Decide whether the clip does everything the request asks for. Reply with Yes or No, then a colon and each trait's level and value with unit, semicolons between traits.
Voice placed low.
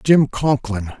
Yes: low, 125 Hz